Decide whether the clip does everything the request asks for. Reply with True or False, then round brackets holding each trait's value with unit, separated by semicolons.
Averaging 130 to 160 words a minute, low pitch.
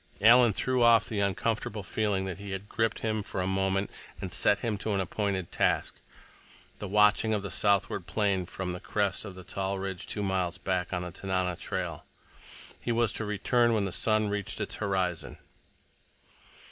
False (175 wpm; 100 Hz)